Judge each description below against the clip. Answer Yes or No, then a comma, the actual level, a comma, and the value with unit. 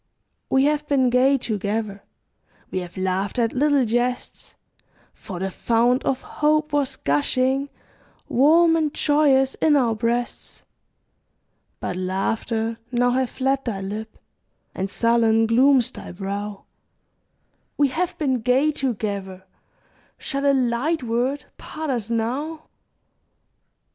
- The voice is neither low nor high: No, high, 245 Hz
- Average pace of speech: No, slow, 120 wpm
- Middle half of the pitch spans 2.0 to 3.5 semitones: No, average, 4.2 semitones